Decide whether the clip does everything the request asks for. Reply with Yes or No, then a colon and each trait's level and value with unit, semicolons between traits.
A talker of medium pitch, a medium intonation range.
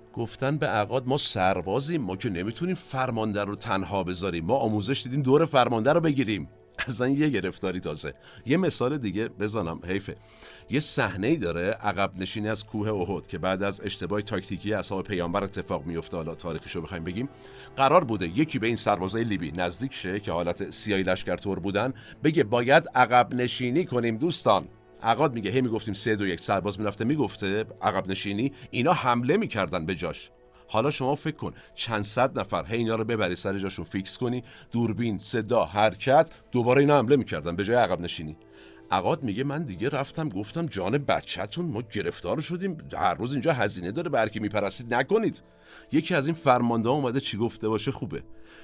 No: low, 110 Hz; average, 5.0 semitones